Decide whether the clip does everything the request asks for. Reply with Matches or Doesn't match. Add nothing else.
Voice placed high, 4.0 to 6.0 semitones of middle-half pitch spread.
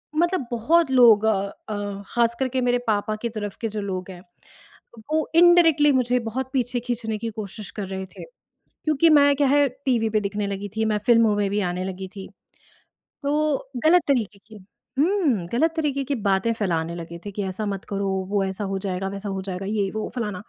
Matches